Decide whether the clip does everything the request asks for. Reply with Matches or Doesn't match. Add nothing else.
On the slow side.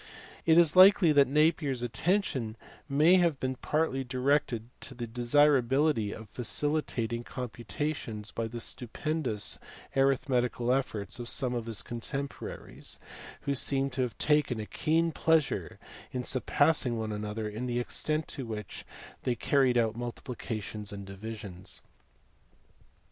Matches